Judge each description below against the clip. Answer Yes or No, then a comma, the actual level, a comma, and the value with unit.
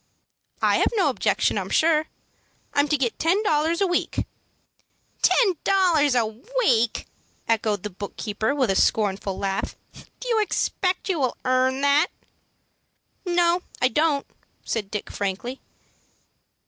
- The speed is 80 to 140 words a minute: Yes, slow, 135 wpm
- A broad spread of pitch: Yes, wide, 7.8 semitones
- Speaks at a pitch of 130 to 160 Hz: No, very high, 280 Hz